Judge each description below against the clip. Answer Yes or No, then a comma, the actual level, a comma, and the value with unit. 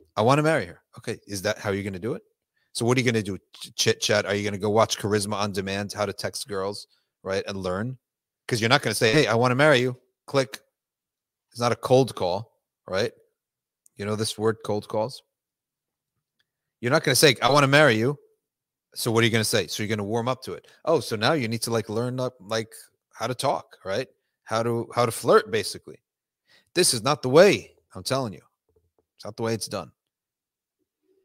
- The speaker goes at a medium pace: No, fast, 235 wpm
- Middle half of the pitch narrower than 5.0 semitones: Yes, average, 3.5 semitones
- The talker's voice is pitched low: Yes, low, 115 Hz